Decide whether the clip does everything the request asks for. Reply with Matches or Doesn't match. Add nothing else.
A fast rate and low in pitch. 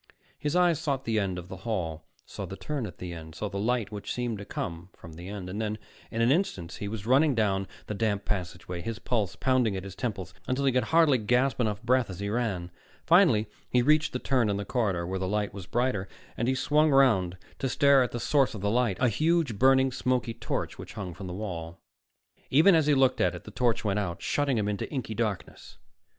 Matches